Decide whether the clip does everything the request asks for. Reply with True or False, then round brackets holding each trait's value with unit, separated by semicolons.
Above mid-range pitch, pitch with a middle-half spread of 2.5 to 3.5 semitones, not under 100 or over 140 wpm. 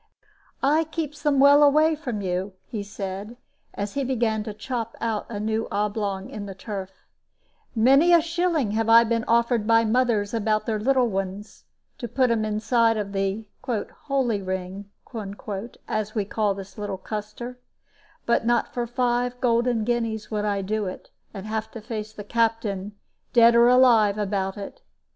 False (220 Hz; 2.9 semitones; 165 wpm)